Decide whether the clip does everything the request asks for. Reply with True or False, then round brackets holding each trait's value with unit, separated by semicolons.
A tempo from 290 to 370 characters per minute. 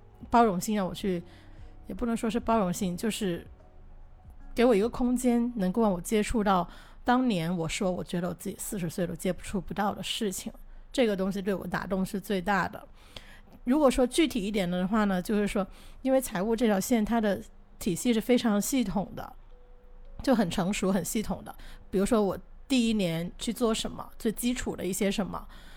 False (275 characters per minute)